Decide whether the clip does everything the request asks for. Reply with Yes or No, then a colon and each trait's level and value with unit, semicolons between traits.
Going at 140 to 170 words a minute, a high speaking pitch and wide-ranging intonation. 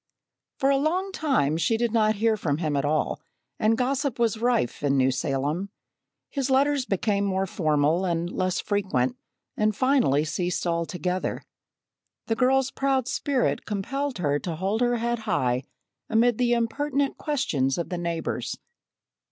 Yes: average, 150 wpm; high, 210 Hz; wide, 7.4 semitones